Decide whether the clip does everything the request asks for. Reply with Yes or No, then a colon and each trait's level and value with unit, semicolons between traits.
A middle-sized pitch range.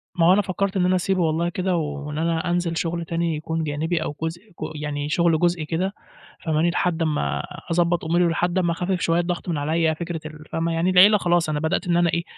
No: narrow, 1.8 semitones